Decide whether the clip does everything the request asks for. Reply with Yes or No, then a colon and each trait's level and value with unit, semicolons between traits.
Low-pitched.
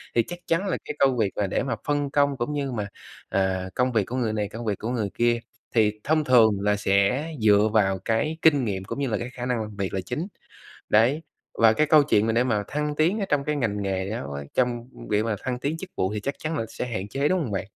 Yes: low, 120 Hz